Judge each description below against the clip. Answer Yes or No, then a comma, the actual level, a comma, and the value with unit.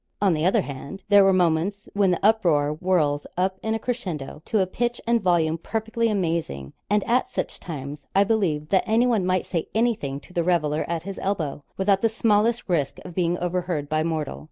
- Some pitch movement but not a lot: Yes, average, 4.7 semitones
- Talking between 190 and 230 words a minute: Yes, average, 200 wpm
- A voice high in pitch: No, medium, 180 Hz